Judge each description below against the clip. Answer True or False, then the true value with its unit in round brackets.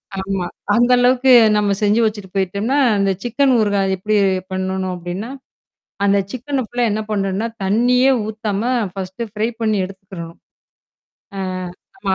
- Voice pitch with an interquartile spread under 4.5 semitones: True (3.5 semitones)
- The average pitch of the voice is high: True (205 Hz)